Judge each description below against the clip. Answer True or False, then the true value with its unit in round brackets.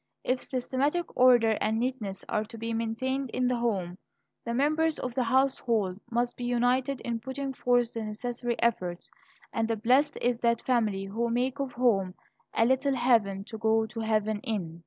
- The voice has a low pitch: False (235 Hz)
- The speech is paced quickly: False (175 wpm)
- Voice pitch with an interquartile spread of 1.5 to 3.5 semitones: True (2.5 semitones)